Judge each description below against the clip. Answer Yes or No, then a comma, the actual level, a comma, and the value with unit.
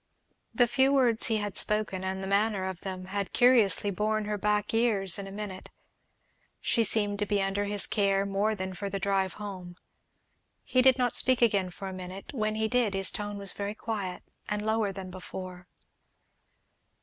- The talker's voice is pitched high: Yes, high, 205 Hz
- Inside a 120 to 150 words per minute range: No, average, 185 wpm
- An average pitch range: No, narrow, 2.1 semitones